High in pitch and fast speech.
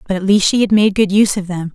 Yes: high, 195 Hz; fast, 345 wpm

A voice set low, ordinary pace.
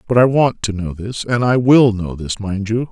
No: low, 110 Hz; fast, 270 wpm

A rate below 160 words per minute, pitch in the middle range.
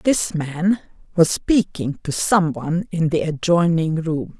Yes: slow, 135 wpm; medium, 165 Hz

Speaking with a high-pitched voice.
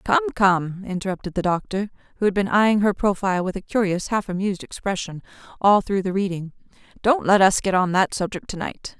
Yes: high, 195 Hz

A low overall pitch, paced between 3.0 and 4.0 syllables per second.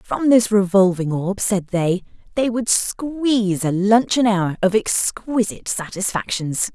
No: high, 205 Hz; 3.9 syllables/s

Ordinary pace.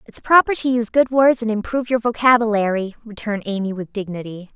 Yes: average, 185 wpm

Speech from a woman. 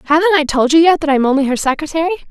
Yes: female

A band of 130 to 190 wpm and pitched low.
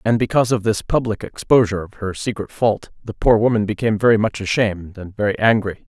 No: average, 200 wpm; low, 105 Hz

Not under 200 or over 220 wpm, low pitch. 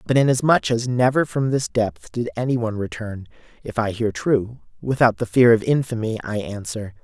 No: average, 190 wpm; low, 120 Hz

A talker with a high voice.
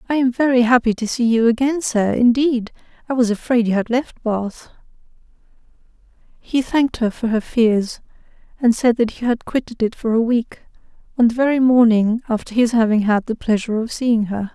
Yes: high, 235 Hz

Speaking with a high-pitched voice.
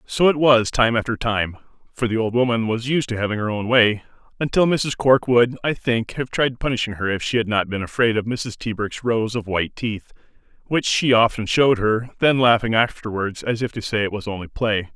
No: low, 115 Hz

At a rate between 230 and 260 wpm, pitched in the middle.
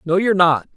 Yes: fast, 235 wpm; medium, 180 Hz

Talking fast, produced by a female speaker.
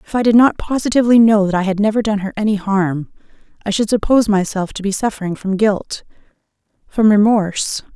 No: average, 190 wpm; female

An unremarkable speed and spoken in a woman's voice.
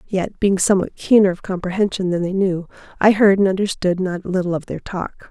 No: fast, 215 wpm; female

